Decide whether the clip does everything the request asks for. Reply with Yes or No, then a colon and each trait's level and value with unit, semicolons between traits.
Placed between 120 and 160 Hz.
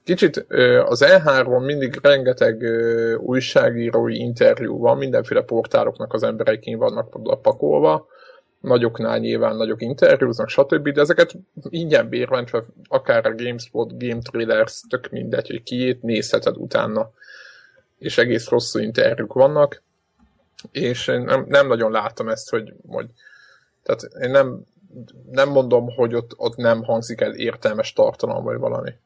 Yes: low, 135 Hz